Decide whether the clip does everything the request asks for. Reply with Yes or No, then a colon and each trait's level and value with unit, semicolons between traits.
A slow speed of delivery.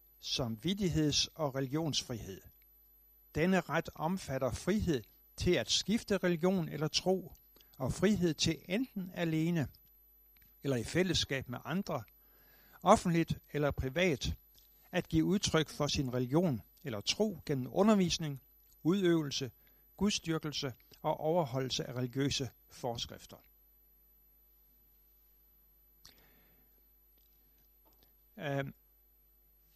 Yes: slow, 90 wpm